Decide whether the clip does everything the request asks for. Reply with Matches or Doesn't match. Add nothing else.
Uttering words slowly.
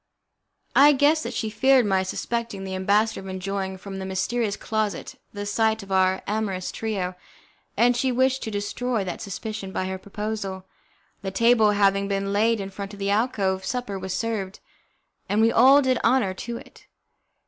Doesn't match